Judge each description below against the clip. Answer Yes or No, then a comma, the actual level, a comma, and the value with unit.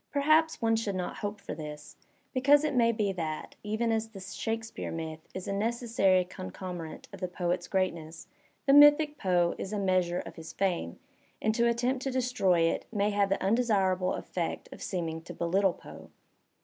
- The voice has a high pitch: Yes, high, 195 Hz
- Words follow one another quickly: No, average, 180 wpm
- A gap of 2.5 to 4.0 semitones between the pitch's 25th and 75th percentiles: No, average, 4.7 semitones